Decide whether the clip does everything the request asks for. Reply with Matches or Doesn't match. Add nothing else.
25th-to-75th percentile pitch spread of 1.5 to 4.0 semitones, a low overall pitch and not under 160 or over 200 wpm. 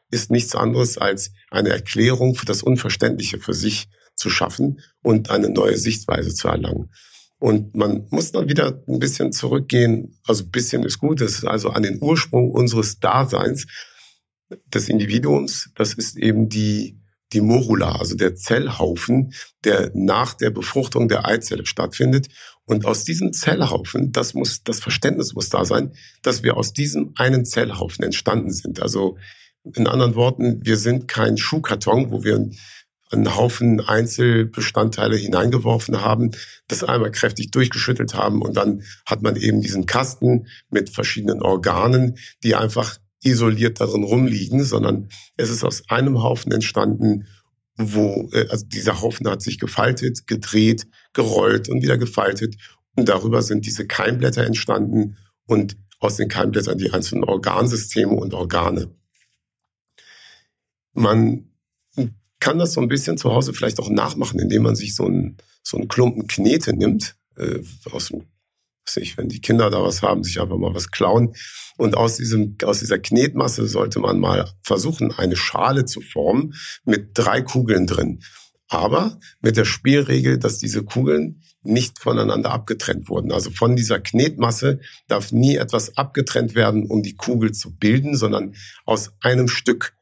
Doesn't match